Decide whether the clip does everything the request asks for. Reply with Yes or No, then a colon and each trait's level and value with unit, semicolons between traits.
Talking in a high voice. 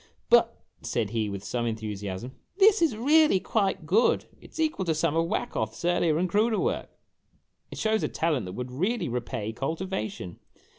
No: medium, 160 Hz